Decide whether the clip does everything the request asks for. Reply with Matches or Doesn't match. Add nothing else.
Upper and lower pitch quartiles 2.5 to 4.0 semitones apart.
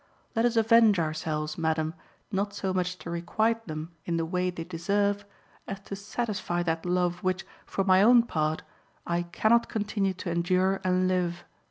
Matches